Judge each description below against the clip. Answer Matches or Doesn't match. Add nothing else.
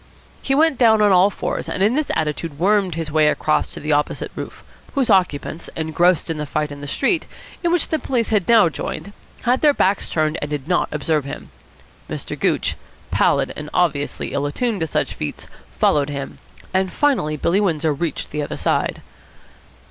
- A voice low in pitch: Doesn't match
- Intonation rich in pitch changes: Matches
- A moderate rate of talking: Matches